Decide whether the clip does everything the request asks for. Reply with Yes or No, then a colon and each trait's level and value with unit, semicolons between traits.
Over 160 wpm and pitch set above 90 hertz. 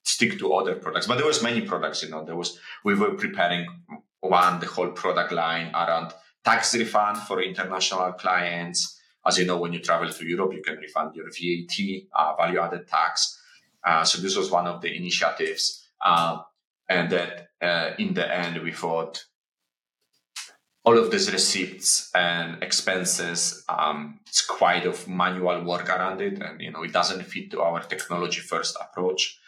No: average, 175 wpm; very low, 85 Hz